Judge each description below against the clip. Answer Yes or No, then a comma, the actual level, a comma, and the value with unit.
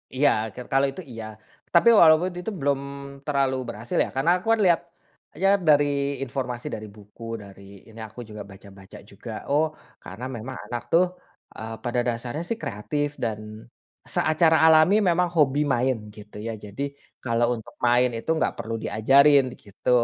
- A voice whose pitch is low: Yes, low, 125 Hz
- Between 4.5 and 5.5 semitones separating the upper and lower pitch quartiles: Yes, average, 5.1 semitones